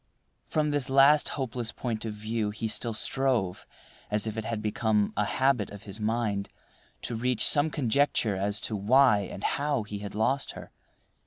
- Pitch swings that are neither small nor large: Yes, average, 4.2 semitones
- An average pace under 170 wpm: No, average, 175 wpm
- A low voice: Yes, low, 110 Hz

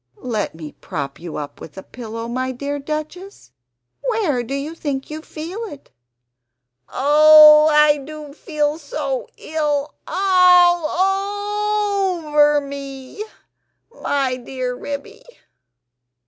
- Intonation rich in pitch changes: No, average, 4.7 semitones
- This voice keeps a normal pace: No, slow, 110 wpm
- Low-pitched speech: No, very high, 300 Hz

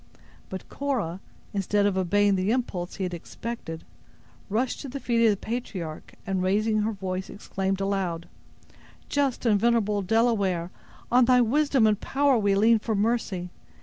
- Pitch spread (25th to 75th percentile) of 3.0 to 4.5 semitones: Yes, average, 3.7 semitones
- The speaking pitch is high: Yes, high, 205 Hz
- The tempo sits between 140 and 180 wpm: Yes, average, 155 wpm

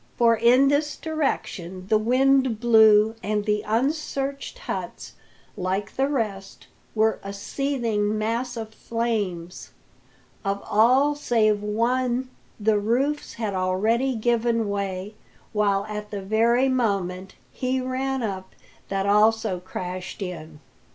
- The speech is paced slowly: Yes, slow, 120 wpm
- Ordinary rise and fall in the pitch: Yes, average, 4.1 semitones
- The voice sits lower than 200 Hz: No, high, 220 Hz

